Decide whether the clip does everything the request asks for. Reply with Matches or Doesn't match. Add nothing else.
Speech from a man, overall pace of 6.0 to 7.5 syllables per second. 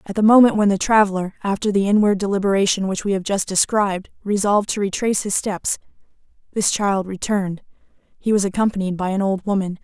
Doesn't match